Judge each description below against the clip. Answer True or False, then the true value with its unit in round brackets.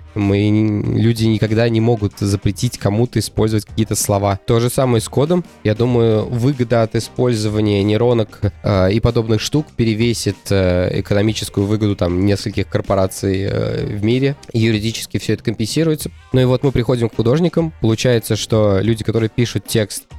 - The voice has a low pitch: True (110 Hz)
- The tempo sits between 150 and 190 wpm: True (155 wpm)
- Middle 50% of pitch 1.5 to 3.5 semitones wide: True (2.9 semitones)